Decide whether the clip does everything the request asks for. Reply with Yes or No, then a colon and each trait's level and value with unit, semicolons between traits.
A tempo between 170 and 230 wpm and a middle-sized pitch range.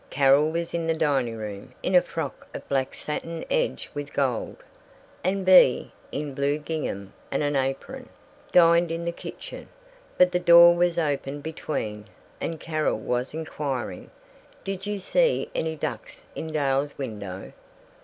No: average, 150 wpm; average, 4.0 semitones